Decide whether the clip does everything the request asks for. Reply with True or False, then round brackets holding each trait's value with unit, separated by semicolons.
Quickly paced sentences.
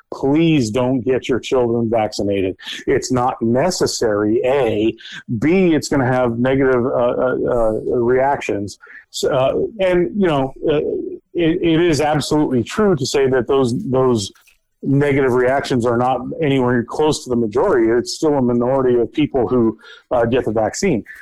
False (155 wpm)